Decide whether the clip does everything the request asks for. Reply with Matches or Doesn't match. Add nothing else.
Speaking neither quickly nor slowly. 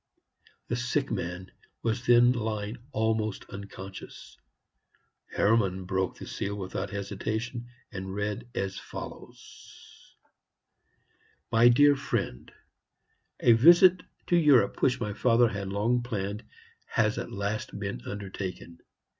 Doesn't match